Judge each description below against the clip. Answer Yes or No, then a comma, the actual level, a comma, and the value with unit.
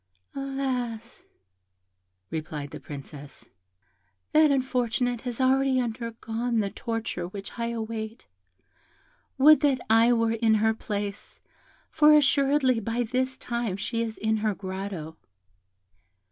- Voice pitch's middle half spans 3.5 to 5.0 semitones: No, average, 3.1 semitones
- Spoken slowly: Yes, slow, 115 wpm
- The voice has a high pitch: Yes, high, 230 Hz